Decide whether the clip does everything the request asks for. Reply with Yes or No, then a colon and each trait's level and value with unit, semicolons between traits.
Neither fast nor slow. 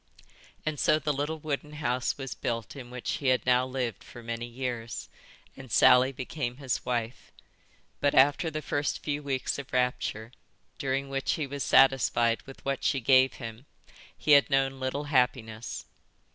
Yes: average, 165 wpm